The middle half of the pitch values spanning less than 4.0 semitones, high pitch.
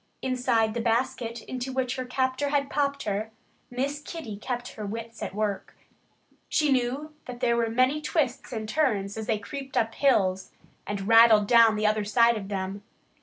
Yes: average, 3.4 semitones; high, 235 Hz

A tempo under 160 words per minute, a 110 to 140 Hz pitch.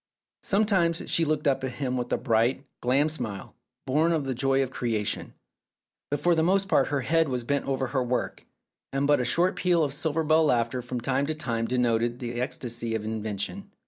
No: fast, 205 wpm; low, 135 Hz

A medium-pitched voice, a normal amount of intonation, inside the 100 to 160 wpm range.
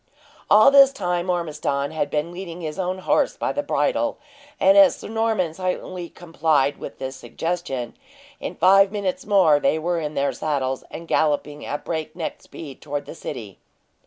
No: medium, 165 Hz; average, 4.0 semitones; average, 170 wpm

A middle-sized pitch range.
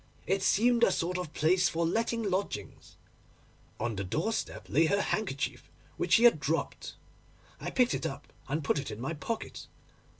No: wide, 6.5 semitones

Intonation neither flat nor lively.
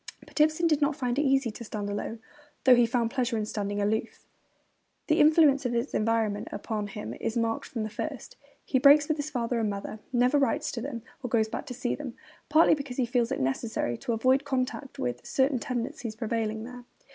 Yes: average, 4.0 semitones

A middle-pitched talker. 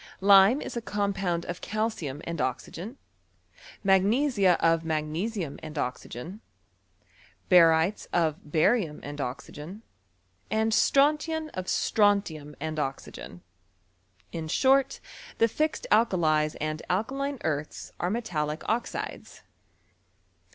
Yes: medium, 180 Hz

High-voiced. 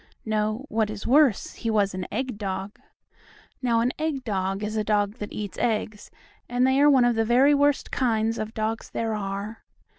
Yes: high, 220 Hz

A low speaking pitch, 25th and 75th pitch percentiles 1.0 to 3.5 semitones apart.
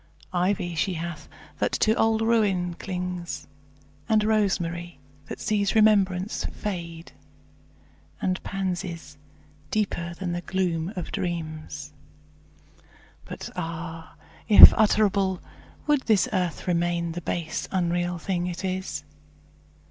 No: medium, 180 Hz; narrow, 2.5 semitones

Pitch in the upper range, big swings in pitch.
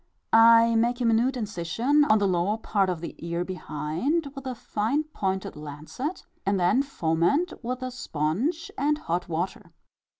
Yes: high, 220 Hz; wide, 6.9 semitones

